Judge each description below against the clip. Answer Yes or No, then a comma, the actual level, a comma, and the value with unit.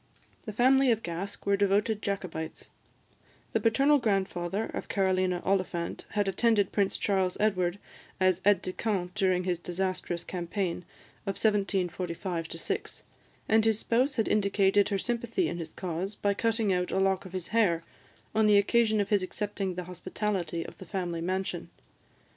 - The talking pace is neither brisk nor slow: Yes, average, 160 wpm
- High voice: Yes, high, 195 Hz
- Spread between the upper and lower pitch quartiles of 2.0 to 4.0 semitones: Yes, average, 2.8 semitones